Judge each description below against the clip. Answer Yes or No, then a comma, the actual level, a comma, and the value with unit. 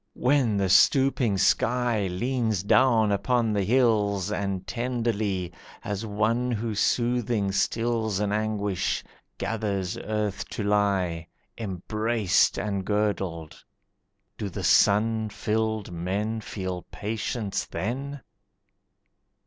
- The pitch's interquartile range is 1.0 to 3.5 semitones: Yes, average, 2.8 semitones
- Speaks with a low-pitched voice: Yes, low, 105 Hz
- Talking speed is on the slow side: Yes, slow, 100 wpm